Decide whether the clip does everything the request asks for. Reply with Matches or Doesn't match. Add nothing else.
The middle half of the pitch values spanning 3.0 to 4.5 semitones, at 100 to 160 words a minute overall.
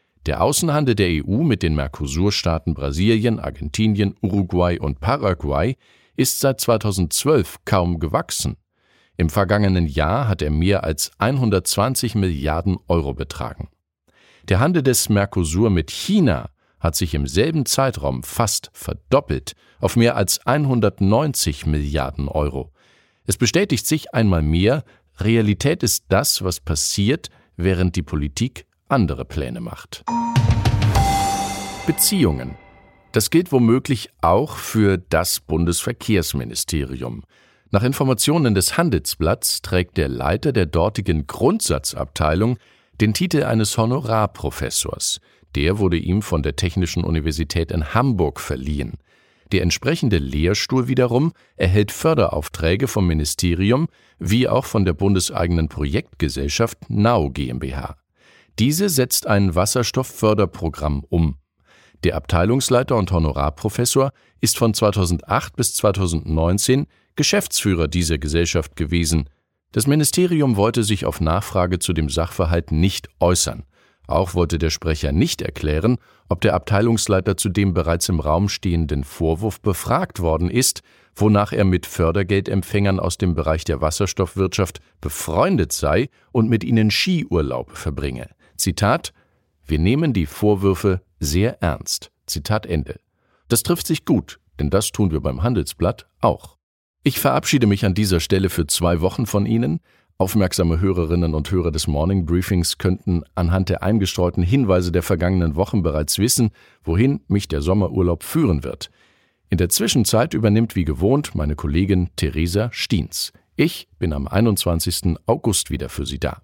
Doesn't match